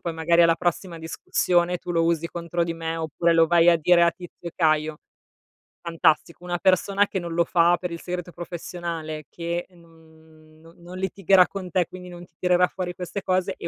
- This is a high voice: No, medium, 170 Hz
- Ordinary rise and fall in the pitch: No, narrow, 1.4 semitones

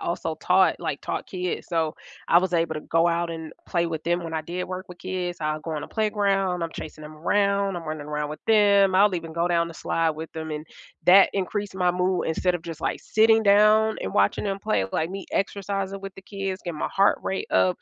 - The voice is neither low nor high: Yes, medium, 175 Hz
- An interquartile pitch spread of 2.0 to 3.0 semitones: No, average, 3.4 semitones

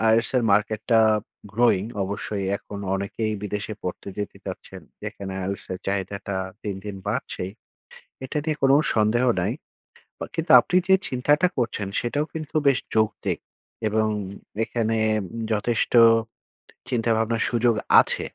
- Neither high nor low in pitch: No, low, 110 Hz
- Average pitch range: Yes, average, 3.0 semitones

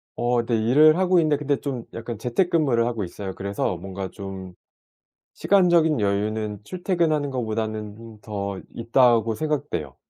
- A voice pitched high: No, low, 115 Hz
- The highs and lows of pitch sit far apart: Yes, wide, 6.5 semitones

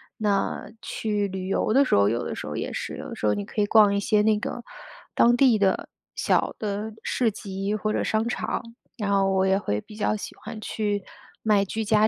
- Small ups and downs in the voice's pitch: Yes, narrow, 1.9 semitones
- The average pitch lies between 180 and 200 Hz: No, high, 210 Hz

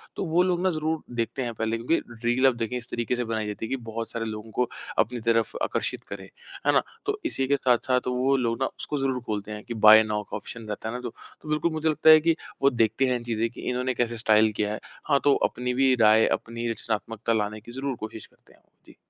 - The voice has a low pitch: Yes, low, 120 Hz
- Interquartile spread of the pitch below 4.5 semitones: Yes, average, 3.2 semitones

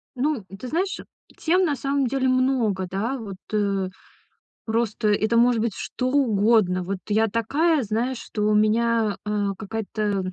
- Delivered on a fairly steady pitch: No, average, 3.7 semitones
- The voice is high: Yes, high, 225 Hz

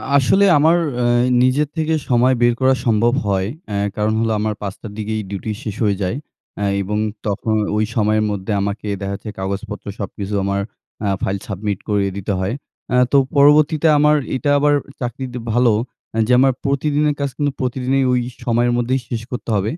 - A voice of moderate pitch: No, low, 115 Hz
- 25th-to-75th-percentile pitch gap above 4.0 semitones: Yes, average, 4.6 semitones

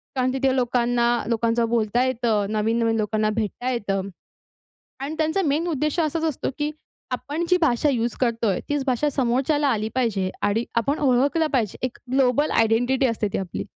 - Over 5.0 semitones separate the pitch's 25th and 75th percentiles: No, average, 3.8 semitones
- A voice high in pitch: Yes, high, 245 Hz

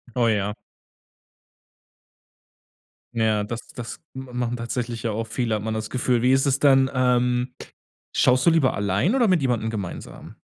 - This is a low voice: Yes, low, 120 Hz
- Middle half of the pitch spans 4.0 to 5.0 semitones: No, average, 2.7 semitones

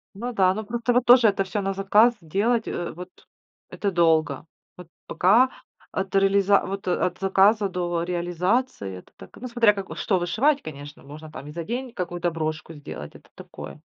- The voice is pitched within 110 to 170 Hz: No, high, 190 Hz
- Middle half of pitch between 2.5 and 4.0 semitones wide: No, average, 4.5 semitones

